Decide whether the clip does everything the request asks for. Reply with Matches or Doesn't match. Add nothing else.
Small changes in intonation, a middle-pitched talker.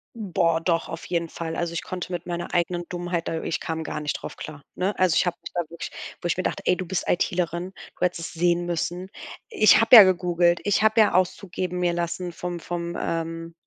Matches